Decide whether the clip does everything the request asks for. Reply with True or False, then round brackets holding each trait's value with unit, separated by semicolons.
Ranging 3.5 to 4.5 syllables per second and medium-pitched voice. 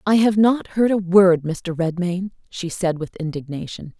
True (4.4 syllables/s; 180 Hz)